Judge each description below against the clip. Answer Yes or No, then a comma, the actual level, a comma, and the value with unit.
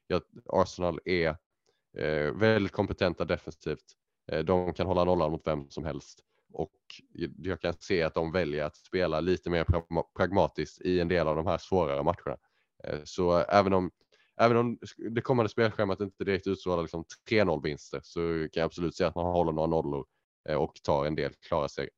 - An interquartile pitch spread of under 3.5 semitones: Yes, average, 2.7 semitones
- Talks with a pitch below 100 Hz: Yes, very low, 90 Hz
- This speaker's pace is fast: No, average, 170 wpm